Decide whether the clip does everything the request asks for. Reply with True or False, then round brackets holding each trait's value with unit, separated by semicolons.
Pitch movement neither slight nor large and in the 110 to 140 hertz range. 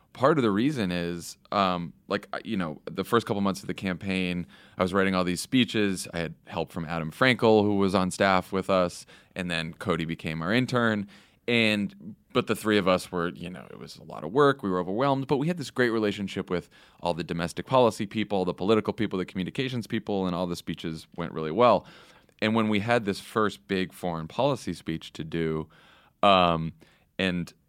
False (3.9 semitones; 95 Hz)